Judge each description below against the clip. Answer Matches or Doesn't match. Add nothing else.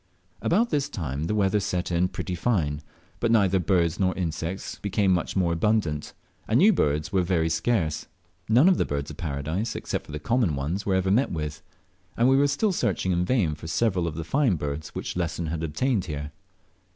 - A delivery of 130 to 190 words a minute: Doesn't match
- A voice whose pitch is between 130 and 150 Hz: Doesn't match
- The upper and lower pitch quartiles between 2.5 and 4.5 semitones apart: Doesn't match